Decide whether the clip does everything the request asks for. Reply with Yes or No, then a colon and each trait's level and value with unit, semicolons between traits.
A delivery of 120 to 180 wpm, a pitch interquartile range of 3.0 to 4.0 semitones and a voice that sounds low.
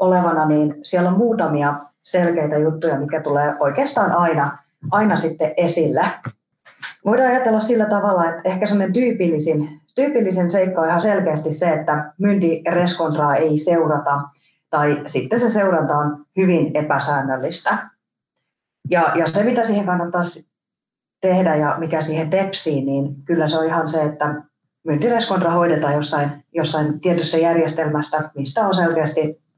No: average, 135 wpm; average, 3.5 semitones; medium, 160 Hz